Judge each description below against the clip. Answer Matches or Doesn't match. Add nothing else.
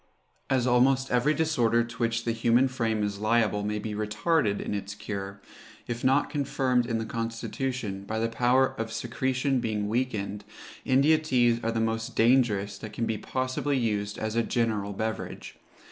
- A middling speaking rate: Matches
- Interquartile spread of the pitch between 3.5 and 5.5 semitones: Doesn't match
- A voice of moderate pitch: Doesn't match